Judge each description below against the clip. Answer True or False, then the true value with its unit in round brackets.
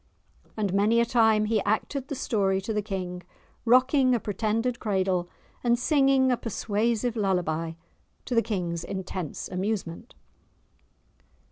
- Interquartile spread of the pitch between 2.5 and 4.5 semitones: True (3.8 semitones)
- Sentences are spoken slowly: True (130 wpm)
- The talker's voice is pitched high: True (215 Hz)